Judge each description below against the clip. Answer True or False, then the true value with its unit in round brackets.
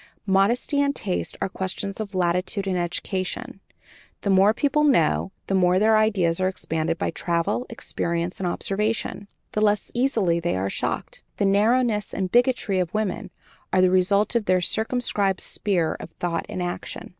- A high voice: True (195 Hz)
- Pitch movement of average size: True (3.2 semitones)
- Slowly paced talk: False (165 wpm)